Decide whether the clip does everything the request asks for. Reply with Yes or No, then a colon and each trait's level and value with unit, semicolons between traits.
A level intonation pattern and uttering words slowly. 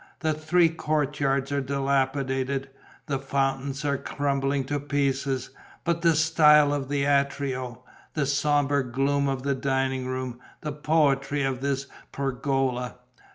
Yes: narrow, 1.4 semitones; slow, 130 wpm